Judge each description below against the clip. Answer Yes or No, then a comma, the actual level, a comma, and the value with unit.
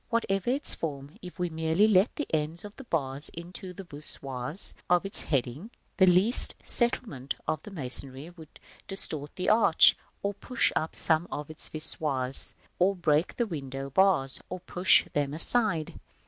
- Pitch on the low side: No, medium, 165 Hz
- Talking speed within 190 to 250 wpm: No, average, 160 wpm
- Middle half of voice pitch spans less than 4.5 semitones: No, average, 5.1 semitones